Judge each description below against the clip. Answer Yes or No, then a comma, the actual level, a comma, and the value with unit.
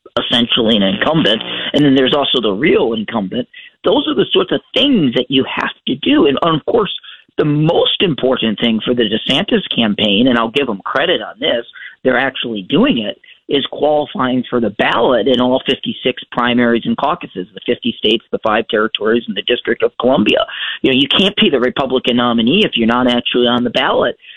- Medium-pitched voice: No, low, 125 Hz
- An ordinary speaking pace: Yes, average, 195 wpm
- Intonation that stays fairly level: No, average, 3.7 semitones